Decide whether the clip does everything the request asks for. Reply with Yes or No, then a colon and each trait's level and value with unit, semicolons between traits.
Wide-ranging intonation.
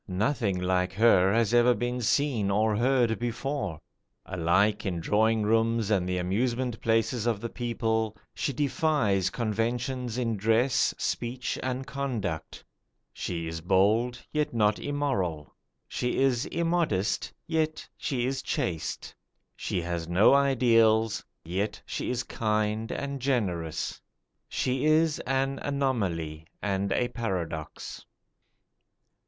No: average, 4.8 semitones